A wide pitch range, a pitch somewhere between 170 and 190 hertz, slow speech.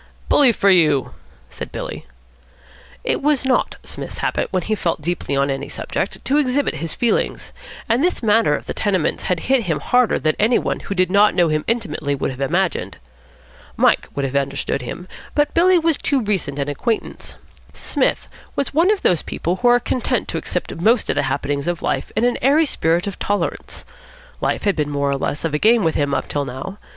No: wide, 8.7 semitones; medium, 185 Hz; fast, 205 wpm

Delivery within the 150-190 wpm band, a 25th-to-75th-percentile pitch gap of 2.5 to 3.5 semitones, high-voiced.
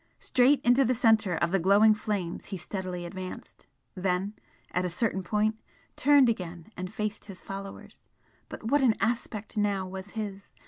Yes: average, 165 wpm; average, 3.1 semitones; high, 200 Hz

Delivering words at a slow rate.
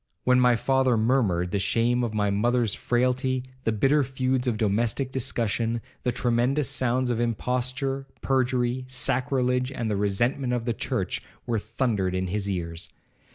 No: average, 155 wpm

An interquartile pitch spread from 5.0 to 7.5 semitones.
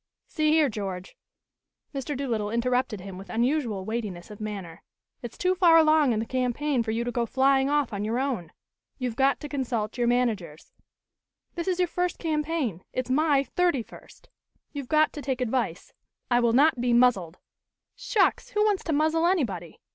Yes: wide, 5.5 semitones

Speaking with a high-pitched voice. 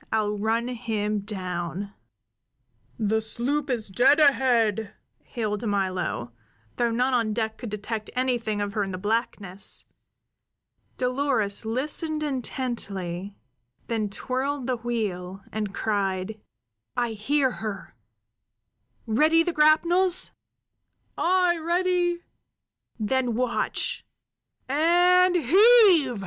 Yes: high, 235 Hz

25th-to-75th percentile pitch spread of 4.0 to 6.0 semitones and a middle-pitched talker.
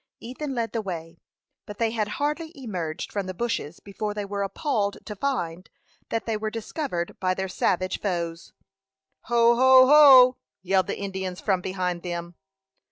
No: average, 4.5 semitones; high, 205 Hz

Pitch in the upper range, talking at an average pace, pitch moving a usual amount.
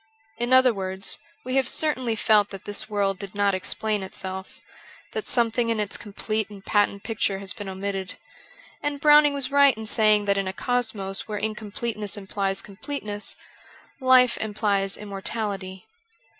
Yes: high, 210 Hz; average, 160 wpm; average, 3.2 semitones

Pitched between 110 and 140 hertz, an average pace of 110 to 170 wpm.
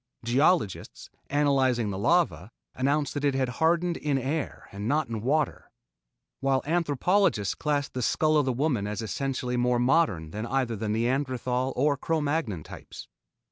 Yes: low, 135 Hz; average, 155 wpm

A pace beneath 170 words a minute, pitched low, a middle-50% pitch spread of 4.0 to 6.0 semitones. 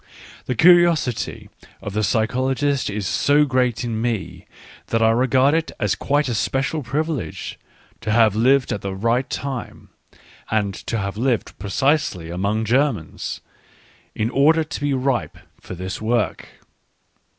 Yes: average, 140 wpm; low, 120 Hz; average, 4.4 semitones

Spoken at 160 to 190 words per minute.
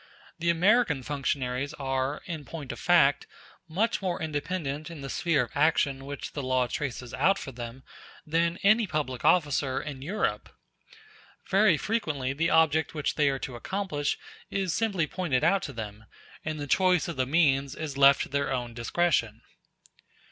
Yes: average, 165 wpm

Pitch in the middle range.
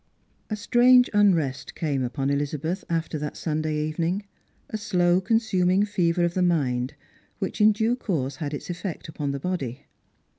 Yes: medium, 170 Hz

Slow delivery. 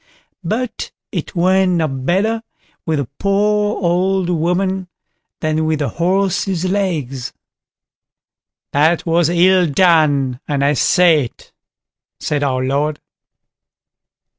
Yes: slow, 110 wpm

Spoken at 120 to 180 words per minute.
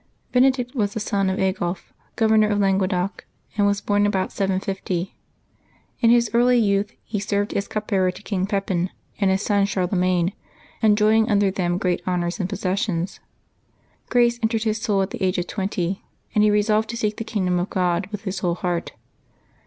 No: average, 190 wpm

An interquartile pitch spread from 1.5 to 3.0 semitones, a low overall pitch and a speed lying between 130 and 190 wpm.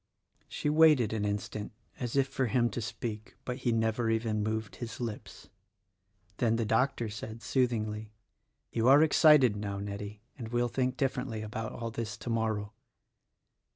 Yes: narrow, 2.6 semitones; low, 115 Hz; average, 160 wpm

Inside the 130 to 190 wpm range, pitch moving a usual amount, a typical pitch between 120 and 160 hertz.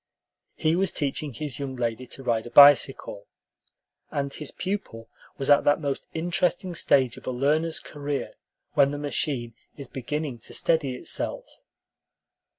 Yes: average, 150 wpm; average, 3.3 semitones; medium, 140 Hz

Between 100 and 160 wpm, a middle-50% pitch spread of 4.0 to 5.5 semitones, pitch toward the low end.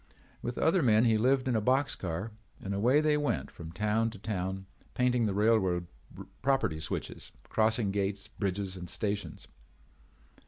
Yes: average, 155 wpm; average, 4.3 semitones; low, 105 Hz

